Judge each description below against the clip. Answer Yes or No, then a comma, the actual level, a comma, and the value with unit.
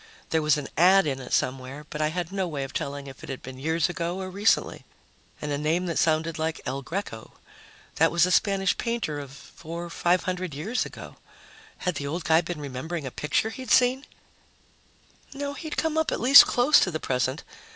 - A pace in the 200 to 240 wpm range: Yes, fast, 205 wpm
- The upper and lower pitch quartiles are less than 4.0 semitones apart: No, average, 4.7 semitones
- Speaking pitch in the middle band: Yes, medium, 165 Hz